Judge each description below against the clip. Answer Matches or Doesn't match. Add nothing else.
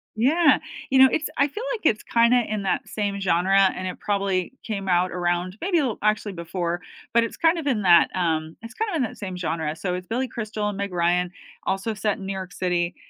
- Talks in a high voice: Matches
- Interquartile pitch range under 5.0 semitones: Matches